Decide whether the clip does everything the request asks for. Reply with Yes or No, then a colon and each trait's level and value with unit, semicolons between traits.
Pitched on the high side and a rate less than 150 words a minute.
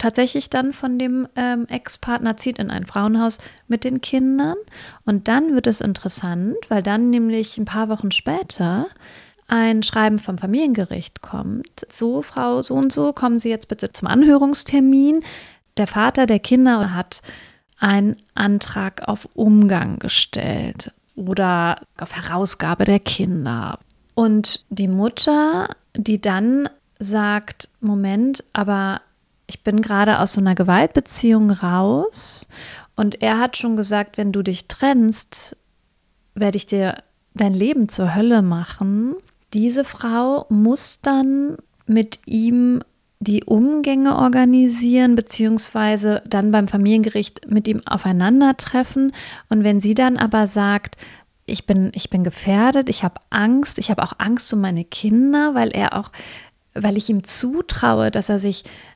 Yes: high, 220 Hz; average, 140 wpm